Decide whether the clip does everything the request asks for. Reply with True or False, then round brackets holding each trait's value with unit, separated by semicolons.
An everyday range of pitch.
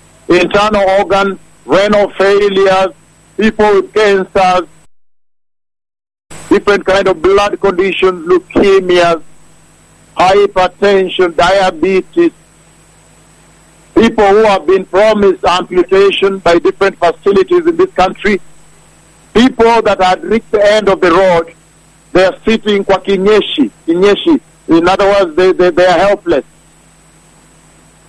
False (2.2 semitones)